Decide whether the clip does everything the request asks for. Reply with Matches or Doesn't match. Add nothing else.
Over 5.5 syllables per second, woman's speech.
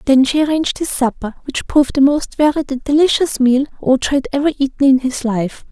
Matches